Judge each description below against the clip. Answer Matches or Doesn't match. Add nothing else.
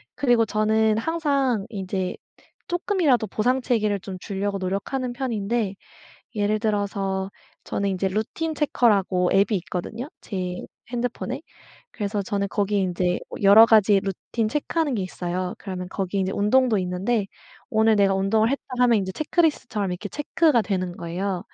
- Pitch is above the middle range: Matches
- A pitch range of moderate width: Matches